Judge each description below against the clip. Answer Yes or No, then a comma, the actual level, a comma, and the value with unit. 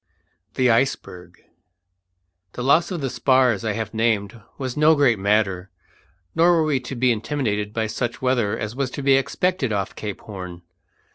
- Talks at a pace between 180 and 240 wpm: No, average, 165 wpm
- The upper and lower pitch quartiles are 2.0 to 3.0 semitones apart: No, average, 4.5 semitones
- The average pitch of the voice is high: No, low, 120 Hz